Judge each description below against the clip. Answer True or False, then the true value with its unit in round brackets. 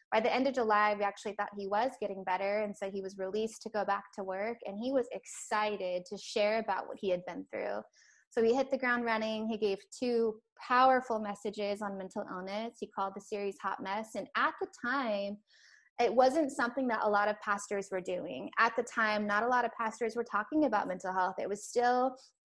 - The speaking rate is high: True (225 wpm)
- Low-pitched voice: False (215 Hz)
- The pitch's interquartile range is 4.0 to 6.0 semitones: False (3.2 semitones)